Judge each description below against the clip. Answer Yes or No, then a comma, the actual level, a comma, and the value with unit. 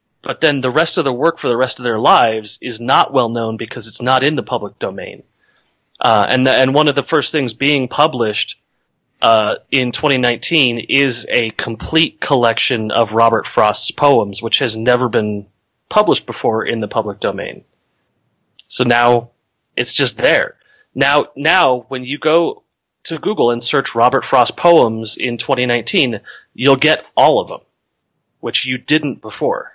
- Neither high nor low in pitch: No, low, 125 Hz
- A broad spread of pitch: No, average, 3.4 semitones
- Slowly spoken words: No, average, 175 wpm